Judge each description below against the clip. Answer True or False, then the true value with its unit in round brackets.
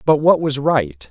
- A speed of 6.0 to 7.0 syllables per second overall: False (4.0 syllables/s)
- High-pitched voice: False (135 Hz)